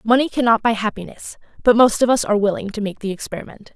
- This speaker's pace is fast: Yes, fast, 225 wpm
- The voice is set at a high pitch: Yes, high, 215 Hz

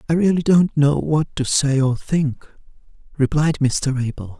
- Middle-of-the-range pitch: Yes, medium, 145 Hz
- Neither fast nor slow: Yes, average, 165 wpm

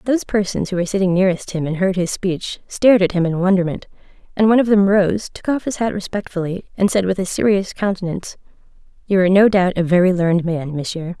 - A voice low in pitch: No, high, 190 Hz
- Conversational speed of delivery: No, fast, 220 wpm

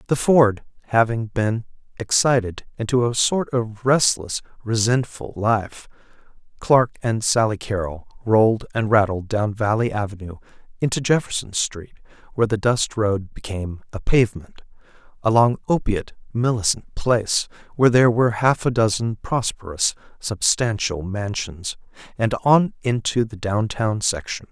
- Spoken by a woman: No, male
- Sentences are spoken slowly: Yes, slow, 125 wpm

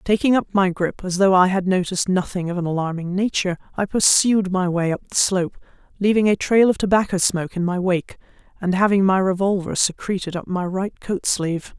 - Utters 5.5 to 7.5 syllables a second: Yes, 5.7 syllables/s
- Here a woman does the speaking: Yes, female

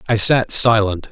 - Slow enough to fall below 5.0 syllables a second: Yes, 4.3 syllables/s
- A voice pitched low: Yes, low, 110 Hz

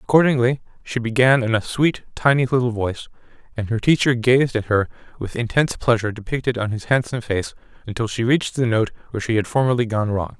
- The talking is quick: No, average, 195 wpm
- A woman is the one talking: No, male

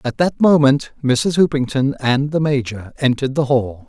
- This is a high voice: No, low, 135 Hz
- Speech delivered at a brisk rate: No, average, 170 wpm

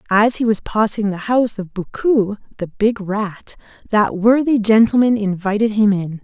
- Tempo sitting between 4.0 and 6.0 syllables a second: Yes, 4.6 syllables/s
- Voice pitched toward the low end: No, high, 215 Hz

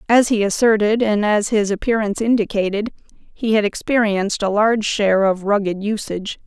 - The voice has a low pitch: No, high, 210 Hz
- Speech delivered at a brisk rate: No, average, 160 wpm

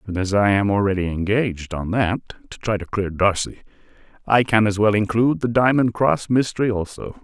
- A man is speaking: Yes, male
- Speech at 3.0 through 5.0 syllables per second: No, 5.6 syllables/s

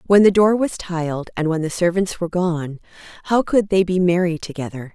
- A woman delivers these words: Yes, female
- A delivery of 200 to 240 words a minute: Yes, fast, 205 wpm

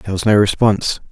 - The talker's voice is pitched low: Yes, low, 100 Hz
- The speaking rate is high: Yes, fast, 215 wpm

